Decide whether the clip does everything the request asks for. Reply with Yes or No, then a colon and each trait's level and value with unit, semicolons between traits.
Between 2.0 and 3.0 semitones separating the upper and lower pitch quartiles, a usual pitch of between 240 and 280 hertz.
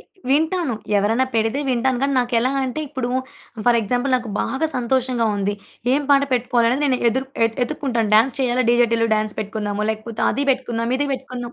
Yes: narrow, 2.5 semitones; high, 245 Hz